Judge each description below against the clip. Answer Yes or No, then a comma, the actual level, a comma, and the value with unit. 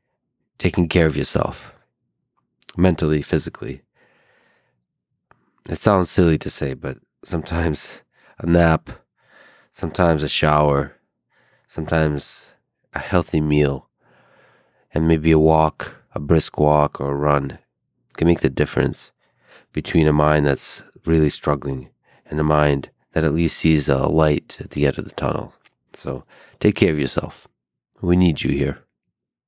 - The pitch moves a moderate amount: No, narrow, 2.1 semitones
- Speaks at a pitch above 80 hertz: No, very low, 75 Hz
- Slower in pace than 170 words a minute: Yes, slow, 135 wpm